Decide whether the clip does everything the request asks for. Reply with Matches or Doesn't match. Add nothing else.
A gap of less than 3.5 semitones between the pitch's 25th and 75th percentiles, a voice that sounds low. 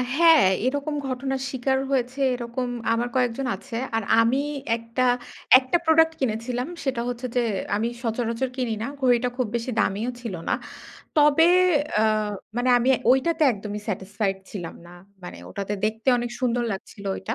Doesn't match